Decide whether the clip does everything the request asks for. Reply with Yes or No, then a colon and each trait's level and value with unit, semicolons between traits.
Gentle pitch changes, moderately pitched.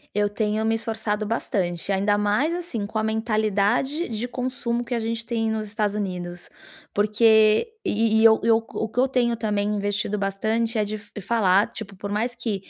No: narrow, 2.0 semitones; high, 220 Hz